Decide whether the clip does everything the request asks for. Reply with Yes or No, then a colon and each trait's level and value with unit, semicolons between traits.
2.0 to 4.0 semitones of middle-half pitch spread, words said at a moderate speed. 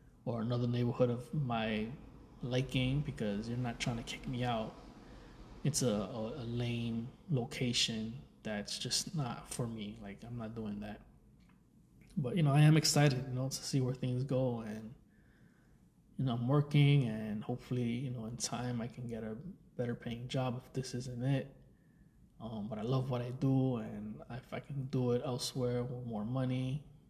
Yes: narrow, 2.4 semitones; average, 180 wpm